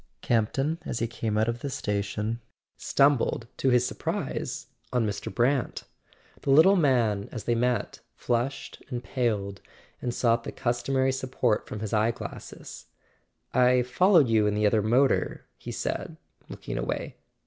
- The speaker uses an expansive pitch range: No, average, 3.3 semitones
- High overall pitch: No, low, 120 Hz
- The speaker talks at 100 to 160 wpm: Yes, average, 150 wpm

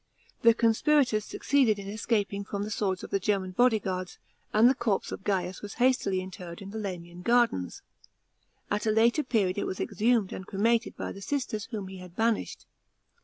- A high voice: Yes, high, 205 Hz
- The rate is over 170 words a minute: Yes, average, 185 wpm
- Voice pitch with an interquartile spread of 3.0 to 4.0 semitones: Yes, average, 3.4 semitones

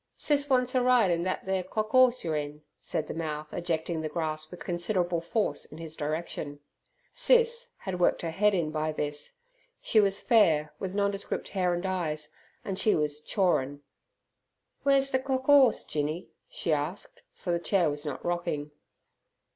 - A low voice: No, medium, 175 Hz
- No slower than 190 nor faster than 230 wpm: No, average, 170 wpm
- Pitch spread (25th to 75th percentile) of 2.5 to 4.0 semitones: No, wide, 5.6 semitones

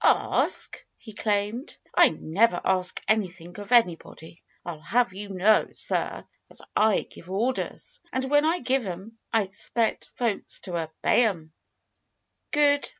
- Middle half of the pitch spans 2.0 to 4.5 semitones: No, average, 4.9 semitones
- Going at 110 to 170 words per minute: Yes, average, 140 wpm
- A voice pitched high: Yes, high, 205 Hz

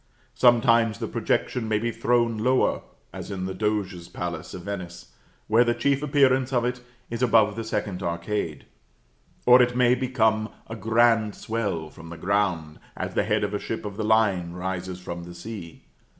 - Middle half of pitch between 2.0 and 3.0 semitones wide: No, average, 4.5 semitones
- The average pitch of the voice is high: No, low, 110 Hz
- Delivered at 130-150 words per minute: No, average, 180 wpm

